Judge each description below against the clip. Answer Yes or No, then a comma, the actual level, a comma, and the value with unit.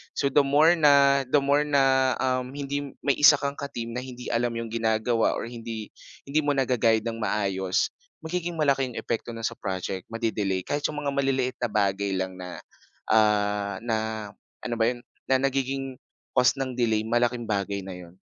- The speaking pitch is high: No, low, 120 Hz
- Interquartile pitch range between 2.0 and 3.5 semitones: No, average, 4.1 semitones